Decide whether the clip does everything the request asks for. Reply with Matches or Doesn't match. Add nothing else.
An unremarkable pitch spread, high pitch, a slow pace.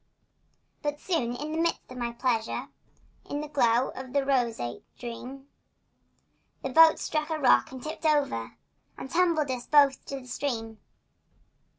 Doesn't match